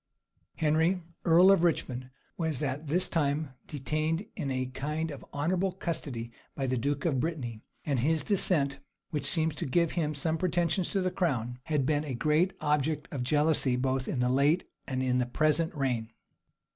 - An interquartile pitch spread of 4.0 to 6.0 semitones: No, average, 3.6 semitones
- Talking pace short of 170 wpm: No, average, 175 wpm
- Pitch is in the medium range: Yes, medium, 150 Hz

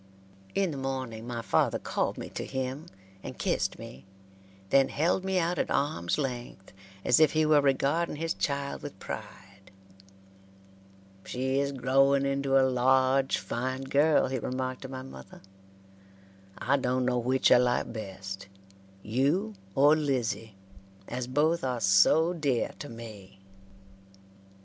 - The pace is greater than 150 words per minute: No, average, 140 wpm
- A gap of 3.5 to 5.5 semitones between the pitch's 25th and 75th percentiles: No, average, 2.8 semitones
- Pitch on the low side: Yes, low, 130 Hz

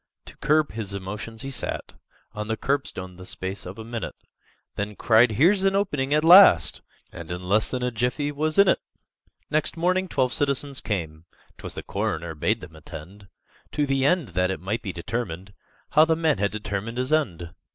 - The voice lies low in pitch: Yes, low, 115 Hz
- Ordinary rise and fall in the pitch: No, wide, 7.5 semitones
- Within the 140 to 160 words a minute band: No, average, 190 wpm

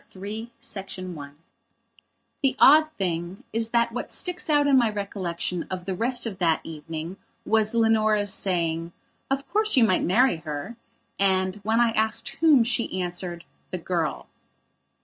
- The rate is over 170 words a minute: No, average, 150 wpm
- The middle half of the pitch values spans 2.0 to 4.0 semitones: No, average, 4.9 semitones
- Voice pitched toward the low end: No, high, 205 Hz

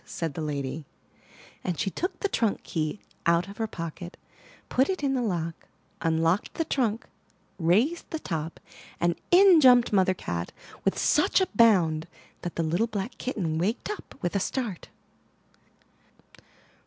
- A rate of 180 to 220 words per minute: No, average, 160 wpm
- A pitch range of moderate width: No, wide, 7.0 semitones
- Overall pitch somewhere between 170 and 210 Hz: Yes, high, 190 Hz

